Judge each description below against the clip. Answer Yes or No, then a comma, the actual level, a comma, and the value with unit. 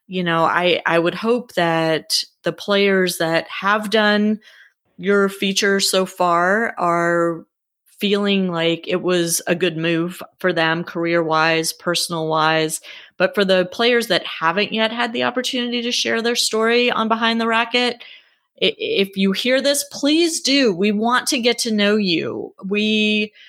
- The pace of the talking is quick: No, average, 160 wpm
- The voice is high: Yes, high, 195 Hz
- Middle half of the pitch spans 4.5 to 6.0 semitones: Yes, average, 5.0 semitones